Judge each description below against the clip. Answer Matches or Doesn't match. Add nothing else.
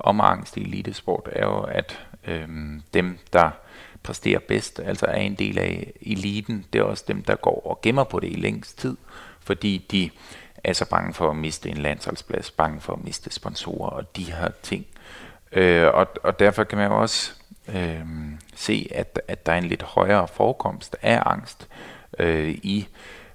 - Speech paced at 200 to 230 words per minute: Doesn't match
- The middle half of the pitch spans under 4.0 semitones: Doesn't match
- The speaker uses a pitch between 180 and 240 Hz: Doesn't match